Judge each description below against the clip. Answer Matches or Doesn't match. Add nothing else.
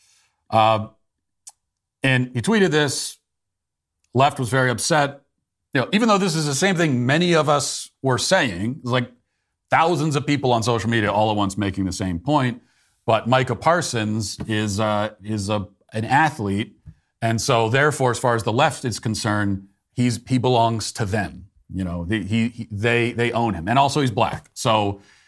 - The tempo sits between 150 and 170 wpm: Doesn't match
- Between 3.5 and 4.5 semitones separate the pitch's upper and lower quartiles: Matches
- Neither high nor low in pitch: Doesn't match